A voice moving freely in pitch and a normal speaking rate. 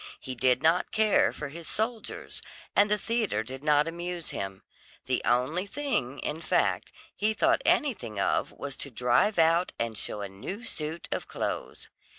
Yes: wide, 8.2 semitones; average, 165 wpm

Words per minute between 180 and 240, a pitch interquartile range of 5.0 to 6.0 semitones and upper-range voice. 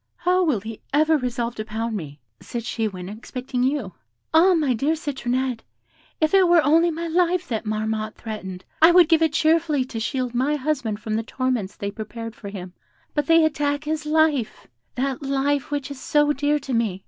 Yes: average, 195 wpm; wide, 5.6 semitones; very high, 265 Hz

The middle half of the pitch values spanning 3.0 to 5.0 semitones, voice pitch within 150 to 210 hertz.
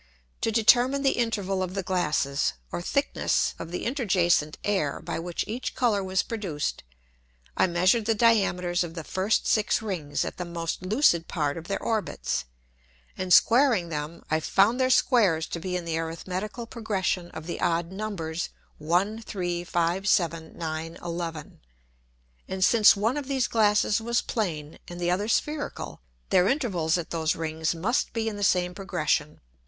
Yes: average, 4.6 semitones; medium, 185 Hz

